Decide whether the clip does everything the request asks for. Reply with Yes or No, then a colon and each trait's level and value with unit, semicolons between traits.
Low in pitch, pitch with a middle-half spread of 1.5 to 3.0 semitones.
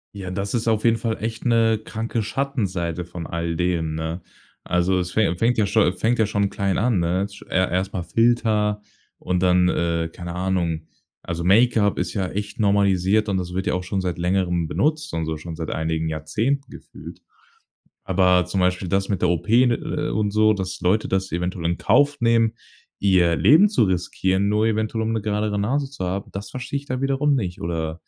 No: very low, 95 Hz; average, 4.0 semitones